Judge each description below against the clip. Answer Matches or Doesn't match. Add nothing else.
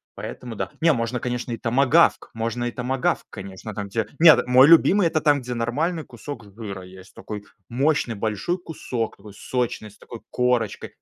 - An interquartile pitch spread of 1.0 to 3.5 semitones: Doesn't match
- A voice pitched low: Matches